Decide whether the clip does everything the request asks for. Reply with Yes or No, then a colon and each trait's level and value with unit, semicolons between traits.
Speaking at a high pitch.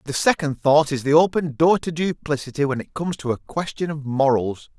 No: medium, 150 Hz